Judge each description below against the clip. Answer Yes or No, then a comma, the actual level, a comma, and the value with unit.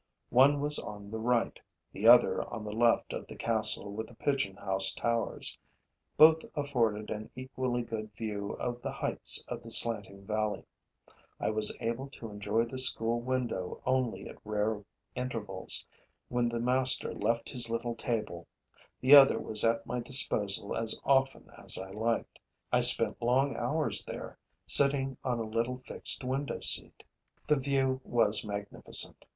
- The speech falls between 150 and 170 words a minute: Yes, average, 155 wpm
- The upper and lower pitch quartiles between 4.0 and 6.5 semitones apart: No, average, 3.3 semitones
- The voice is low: Yes, low, 115 Hz